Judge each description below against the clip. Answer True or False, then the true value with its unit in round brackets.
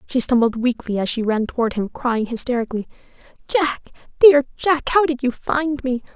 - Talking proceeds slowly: False (175 wpm)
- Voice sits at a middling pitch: False (255 Hz)